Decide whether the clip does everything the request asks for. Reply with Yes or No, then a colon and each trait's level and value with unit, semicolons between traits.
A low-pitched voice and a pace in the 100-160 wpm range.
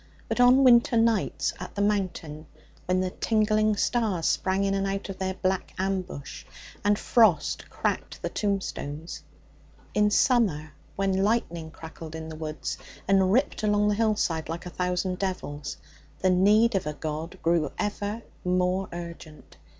No: high, 190 Hz; average, 150 wpm